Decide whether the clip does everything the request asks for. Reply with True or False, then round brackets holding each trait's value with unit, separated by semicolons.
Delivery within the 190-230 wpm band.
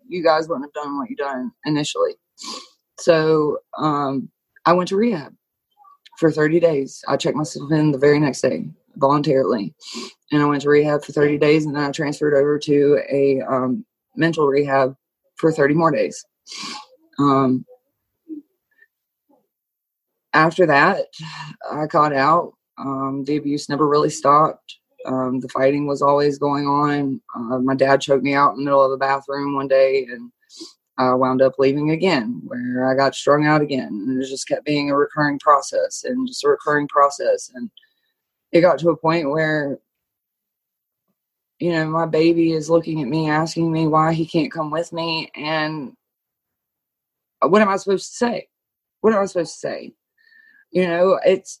False (170 wpm)